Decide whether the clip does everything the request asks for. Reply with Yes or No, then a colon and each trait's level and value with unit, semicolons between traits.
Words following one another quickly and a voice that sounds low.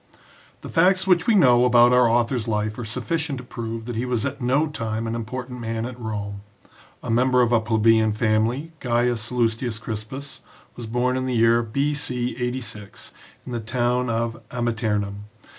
No: average, 175 wpm; low, 120 Hz